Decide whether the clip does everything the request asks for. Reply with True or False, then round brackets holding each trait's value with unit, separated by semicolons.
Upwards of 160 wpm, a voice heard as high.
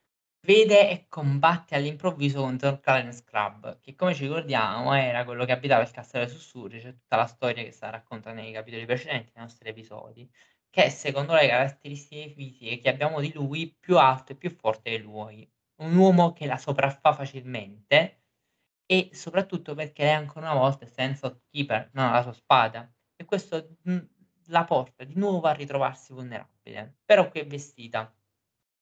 False (170 wpm; 135 Hz)